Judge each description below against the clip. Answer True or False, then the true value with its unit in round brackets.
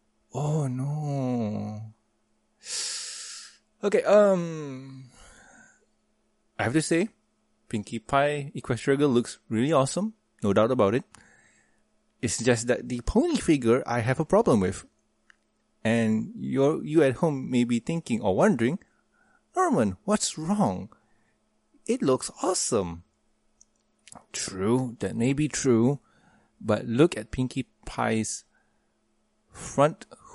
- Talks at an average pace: False (115 wpm)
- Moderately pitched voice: False (130 Hz)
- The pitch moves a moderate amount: False (6.4 semitones)